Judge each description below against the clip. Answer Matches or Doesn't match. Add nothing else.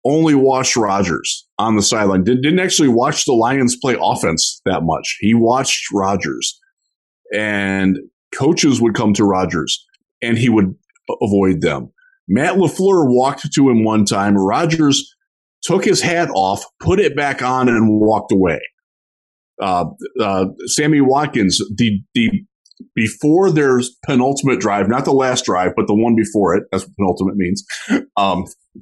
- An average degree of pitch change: Doesn't match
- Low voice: Matches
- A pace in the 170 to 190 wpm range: Doesn't match